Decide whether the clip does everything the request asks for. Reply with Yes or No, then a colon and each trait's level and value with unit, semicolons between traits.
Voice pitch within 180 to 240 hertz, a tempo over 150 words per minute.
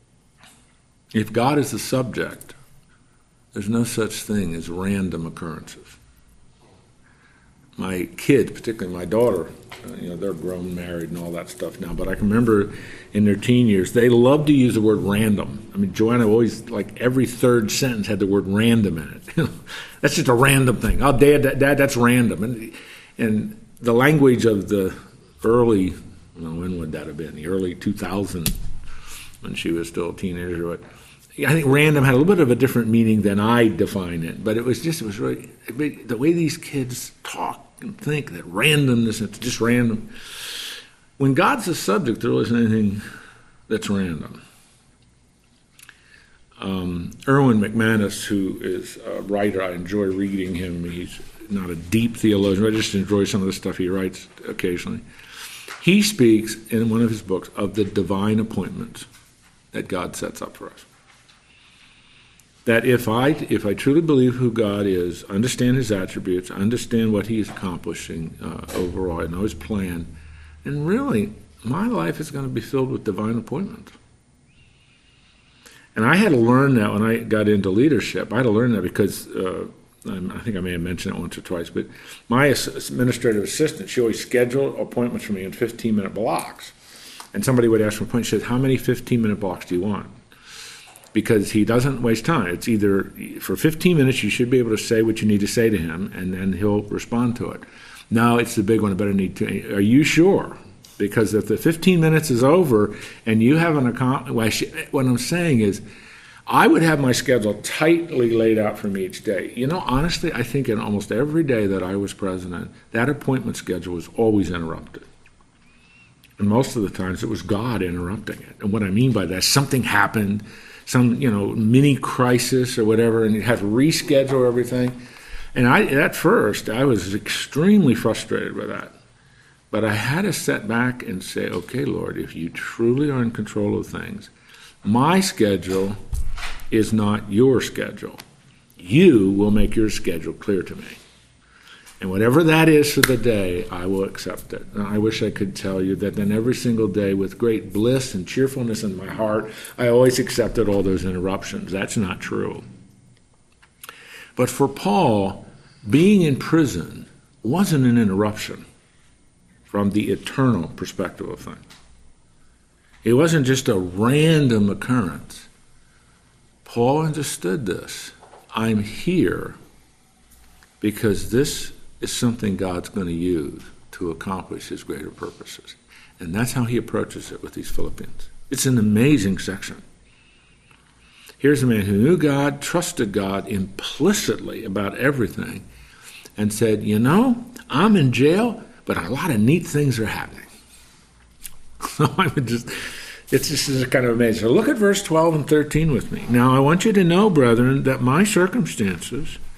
No: low, 110 Hz; average, 170 wpm